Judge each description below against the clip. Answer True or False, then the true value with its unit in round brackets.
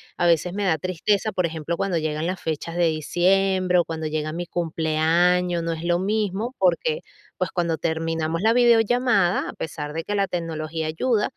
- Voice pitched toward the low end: False (175 Hz)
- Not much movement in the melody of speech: False (3.2 semitones)